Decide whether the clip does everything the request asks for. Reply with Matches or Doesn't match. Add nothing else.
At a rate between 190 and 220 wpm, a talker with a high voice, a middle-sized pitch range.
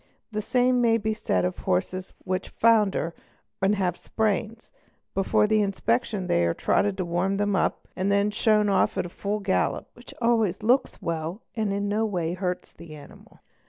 Matches